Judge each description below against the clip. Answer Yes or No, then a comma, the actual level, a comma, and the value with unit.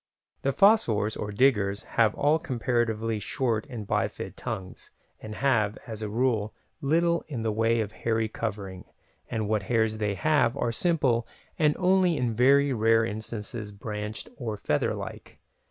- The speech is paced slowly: No, average, 155 wpm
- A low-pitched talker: Yes, low, 115 Hz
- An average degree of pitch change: Yes, average, 3.8 semitones